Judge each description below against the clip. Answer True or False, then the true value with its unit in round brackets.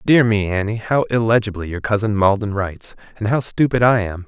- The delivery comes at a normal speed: True (195 wpm)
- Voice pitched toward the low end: True (105 Hz)